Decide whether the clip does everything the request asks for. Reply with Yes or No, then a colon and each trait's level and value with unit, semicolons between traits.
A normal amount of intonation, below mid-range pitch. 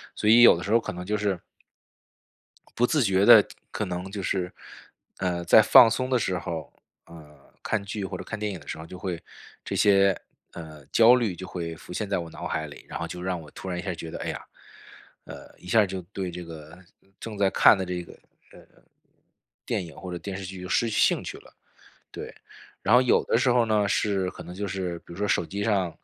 Yes: average, 3.2 semitones; very low, 95 Hz